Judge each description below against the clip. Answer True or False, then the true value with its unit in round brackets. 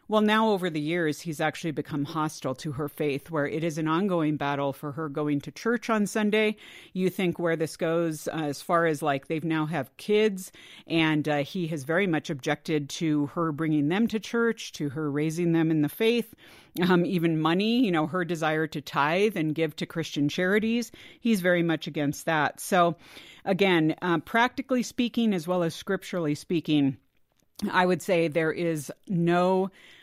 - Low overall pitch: False (165 Hz)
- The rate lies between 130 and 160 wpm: False (190 wpm)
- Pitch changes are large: False (3.7 semitones)